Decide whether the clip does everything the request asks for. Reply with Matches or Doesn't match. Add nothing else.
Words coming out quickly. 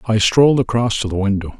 Matches